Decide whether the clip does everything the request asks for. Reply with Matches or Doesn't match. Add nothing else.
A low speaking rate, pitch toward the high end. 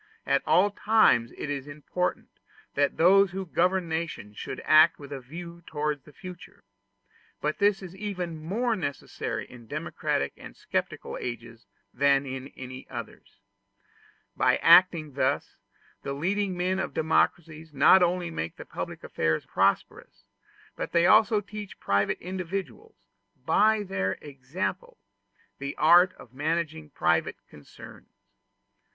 Doesn't match